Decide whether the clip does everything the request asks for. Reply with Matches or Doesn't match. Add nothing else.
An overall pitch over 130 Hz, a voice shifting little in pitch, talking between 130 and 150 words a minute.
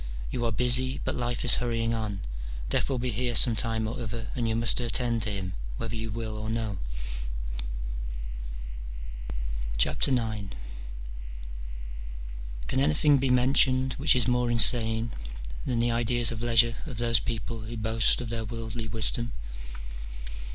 Doesn't match